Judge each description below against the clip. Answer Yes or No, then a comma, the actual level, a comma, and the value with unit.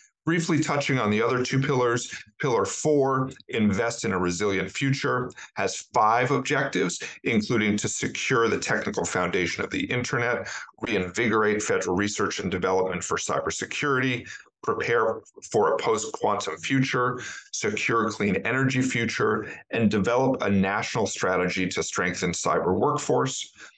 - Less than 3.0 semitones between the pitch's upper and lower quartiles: No, wide, 5.4 semitones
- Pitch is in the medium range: No, low, 120 Hz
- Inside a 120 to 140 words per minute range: Yes, slow, 135 wpm